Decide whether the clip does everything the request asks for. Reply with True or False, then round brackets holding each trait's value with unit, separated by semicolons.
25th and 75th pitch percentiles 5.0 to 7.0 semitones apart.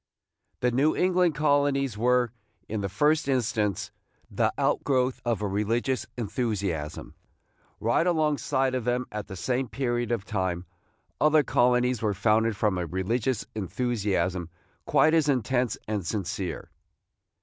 False (4.4 semitones)